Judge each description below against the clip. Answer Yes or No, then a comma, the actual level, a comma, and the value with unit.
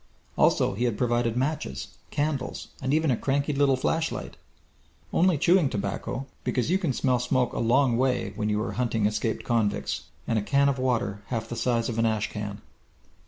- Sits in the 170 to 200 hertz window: No, low, 125 Hz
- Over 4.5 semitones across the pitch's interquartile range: No, average, 3.8 semitones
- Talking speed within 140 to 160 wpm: No, average, 185 wpm